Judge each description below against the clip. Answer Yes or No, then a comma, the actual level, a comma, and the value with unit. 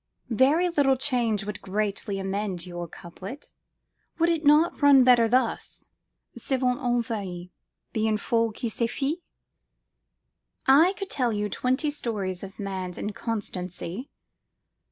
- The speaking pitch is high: Yes, high, 230 Hz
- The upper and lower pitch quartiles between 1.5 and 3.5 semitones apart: No, wide, 5.4 semitones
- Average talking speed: No, slow, 120 wpm